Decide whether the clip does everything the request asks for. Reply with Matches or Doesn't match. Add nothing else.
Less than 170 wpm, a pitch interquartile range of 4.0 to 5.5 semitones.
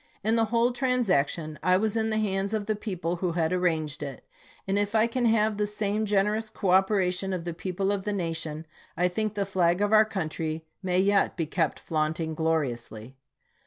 Doesn't match